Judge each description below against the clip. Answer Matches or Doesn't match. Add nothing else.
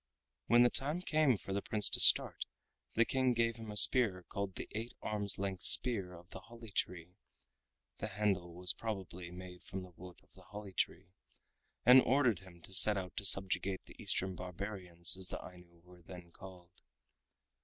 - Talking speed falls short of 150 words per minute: Doesn't match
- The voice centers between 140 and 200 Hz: Doesn't match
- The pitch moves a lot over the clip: Doesn't match